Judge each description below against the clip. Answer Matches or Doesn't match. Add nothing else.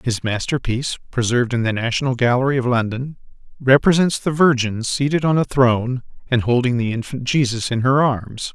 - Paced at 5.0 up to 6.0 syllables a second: Matches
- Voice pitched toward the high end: Doesn't match